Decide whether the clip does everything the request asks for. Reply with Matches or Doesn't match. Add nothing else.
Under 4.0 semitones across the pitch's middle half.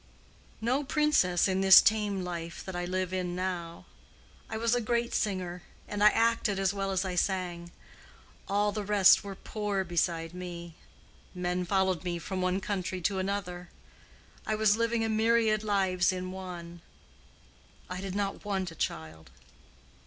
Matches